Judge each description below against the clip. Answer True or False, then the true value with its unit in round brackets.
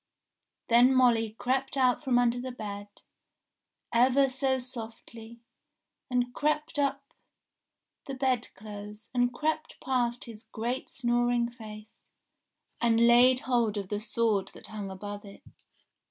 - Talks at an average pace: False (125 wpm)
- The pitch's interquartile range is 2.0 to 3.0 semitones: True (2.7 semitones)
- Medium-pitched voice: False (240 Hz)